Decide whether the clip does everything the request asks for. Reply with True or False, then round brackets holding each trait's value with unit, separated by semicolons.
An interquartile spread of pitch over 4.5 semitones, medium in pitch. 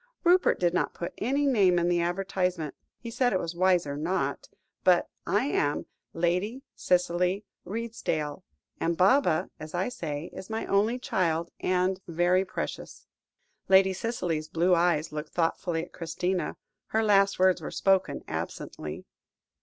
False (2.7 semitones; 180 Hz)